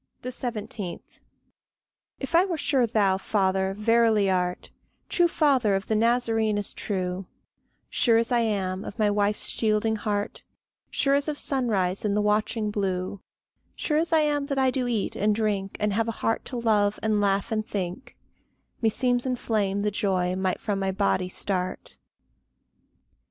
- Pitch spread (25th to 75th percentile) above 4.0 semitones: No, average, 3.4 semitones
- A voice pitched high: Yes, high, 210 Hz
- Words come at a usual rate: Yes, average, 160 wpm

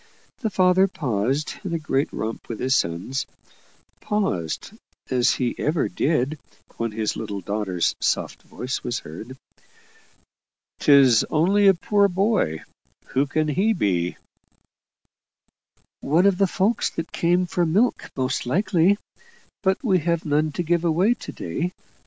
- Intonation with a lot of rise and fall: Yes, wide, 7.2 semitones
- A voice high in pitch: No, medium, 155 Hz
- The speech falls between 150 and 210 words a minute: No, average, 140 wpm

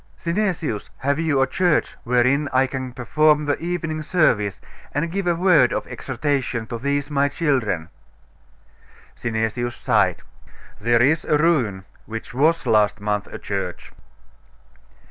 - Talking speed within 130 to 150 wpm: Yes, slow, 135 wpm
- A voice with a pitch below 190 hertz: Yes, low, 135 Hz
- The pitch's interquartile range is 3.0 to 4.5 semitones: No, wide, 5.6 semitones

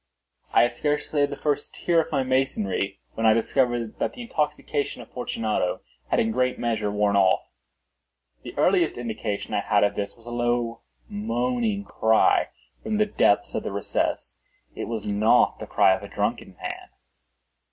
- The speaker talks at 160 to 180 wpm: Yes, average, 175 wpm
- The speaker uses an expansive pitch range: No, average, 3.8 semitones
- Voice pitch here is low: Yes, low, 115 Hz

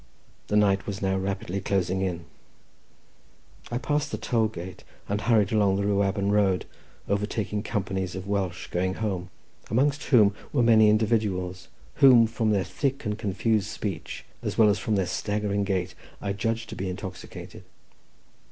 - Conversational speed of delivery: Yes, average, 155 wpm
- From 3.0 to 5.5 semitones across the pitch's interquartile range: No, narrow, 2.4 semitones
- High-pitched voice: No, low, 100 Hz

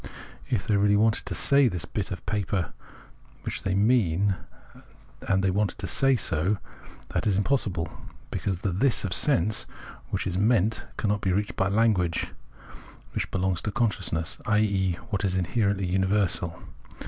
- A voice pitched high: No, low, 100 Hz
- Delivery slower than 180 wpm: Yes, average, 160 wpm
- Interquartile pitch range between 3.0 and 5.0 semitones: No, narrow, 2.5 semitones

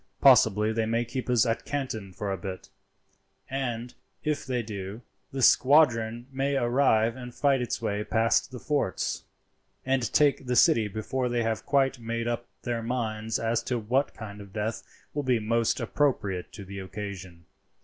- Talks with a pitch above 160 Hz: No, low, 115 Hz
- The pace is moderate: Yes, average, 170 wpm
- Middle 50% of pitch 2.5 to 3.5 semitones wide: Yes, average, 3.1 semitones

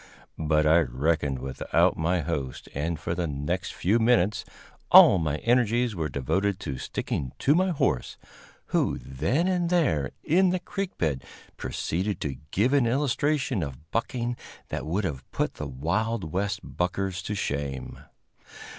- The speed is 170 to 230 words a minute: No, average, 150 wpm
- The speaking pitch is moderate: No, very low, 90 Hz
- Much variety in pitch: Yes, wide, 8.2 semitones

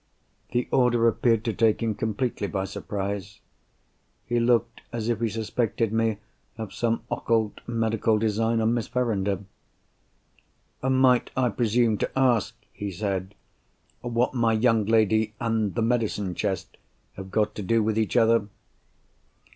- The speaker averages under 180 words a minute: Yes, average, 140 wpm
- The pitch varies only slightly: Yes, narrow, 2.0 semitones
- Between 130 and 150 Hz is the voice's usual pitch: No, low, 110 Hz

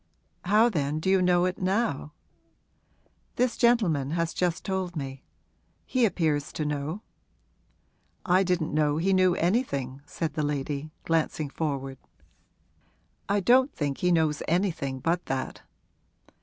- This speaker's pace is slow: Yes, slow, 130 wpm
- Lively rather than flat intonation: No, average, 4.4 semitones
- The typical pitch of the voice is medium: Yes, medium, 165 Hz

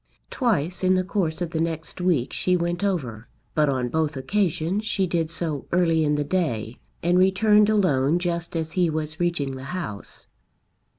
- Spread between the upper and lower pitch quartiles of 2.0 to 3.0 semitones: No, average, 3.6 semitones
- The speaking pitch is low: No, medium, 170 Hz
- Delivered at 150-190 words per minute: Yes, average, 175 wpm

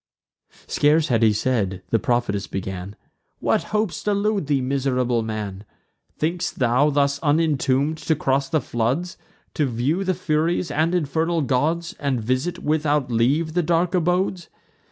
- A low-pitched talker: No, medium, 145 Hz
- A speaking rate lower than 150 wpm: Yes, average, 140 wpm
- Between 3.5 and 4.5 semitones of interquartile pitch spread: No, average, 5.2 semitones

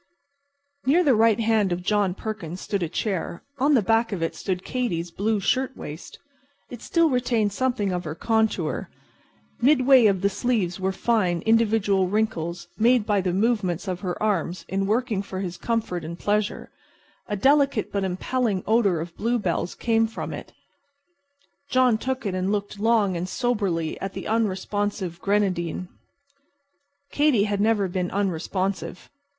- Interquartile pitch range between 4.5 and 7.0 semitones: No, average, 3.7 semitones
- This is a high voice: Yes, high, 205 Hz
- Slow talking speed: No, average, 155 wpm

